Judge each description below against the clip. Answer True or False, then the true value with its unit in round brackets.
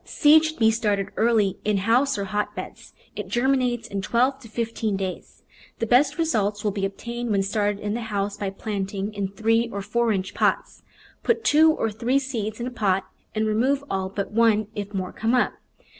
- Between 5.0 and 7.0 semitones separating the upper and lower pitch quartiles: False (3.1 semitones)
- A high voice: True (220 Hz)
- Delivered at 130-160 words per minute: False (200 wpm)